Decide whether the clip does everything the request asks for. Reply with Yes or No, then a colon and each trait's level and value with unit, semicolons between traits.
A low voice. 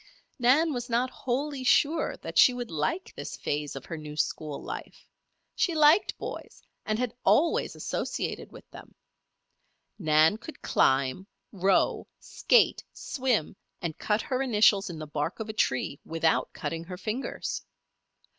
No: high, 215 Hz